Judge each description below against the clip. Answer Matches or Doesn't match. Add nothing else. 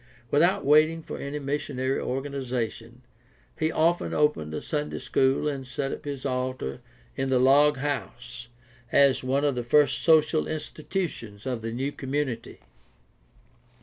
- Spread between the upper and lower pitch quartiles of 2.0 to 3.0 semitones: Matches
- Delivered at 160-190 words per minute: Doesn't match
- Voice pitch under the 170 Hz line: Matches